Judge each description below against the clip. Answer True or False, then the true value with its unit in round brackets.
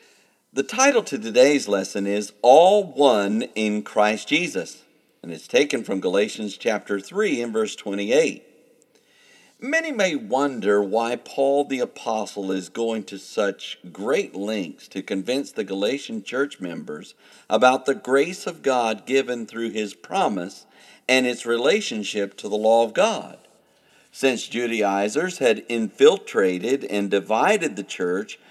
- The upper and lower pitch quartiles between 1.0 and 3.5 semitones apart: False (5.4 semitones)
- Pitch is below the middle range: True (115 Hz)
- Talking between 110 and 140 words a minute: True (135 wpm)